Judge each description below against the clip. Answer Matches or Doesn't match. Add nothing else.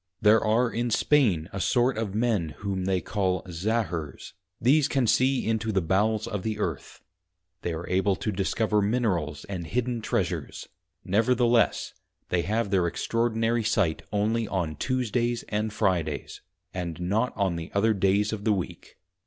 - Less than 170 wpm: Matches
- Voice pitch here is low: Matches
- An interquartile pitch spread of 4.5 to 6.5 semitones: Doesn't match